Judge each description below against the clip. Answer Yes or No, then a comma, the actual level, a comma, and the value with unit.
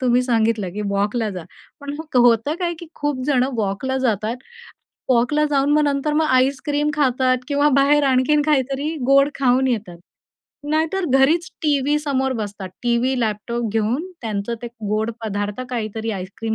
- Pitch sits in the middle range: No, very high, 255 Hz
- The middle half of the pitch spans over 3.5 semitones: Yes, average, 4.5 semitones